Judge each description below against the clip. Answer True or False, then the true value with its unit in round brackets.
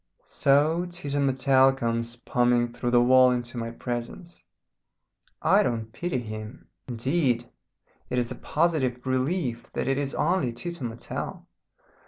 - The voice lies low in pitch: True (125 Hz)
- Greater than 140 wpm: False (135 wpm)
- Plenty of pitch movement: False (2.9 semitones)